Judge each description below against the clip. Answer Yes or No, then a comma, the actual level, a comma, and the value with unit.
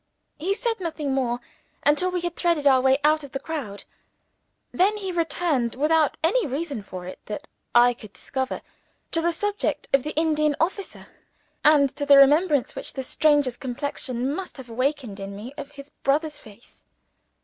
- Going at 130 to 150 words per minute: No, average, 170 wpm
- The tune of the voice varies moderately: Yes, average, 4.1 semitones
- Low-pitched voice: No, very high, 290 Hz